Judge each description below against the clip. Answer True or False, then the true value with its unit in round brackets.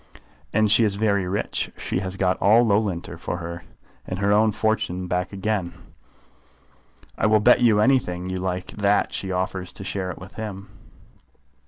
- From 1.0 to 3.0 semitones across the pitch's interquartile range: True (2.6 semitones)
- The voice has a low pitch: True (100 Hz)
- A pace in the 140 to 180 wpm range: True (175 wpm)